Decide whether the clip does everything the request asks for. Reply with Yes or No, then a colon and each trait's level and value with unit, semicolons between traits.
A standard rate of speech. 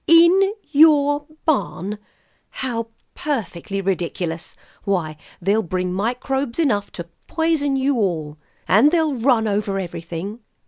No: slow, 110 wpm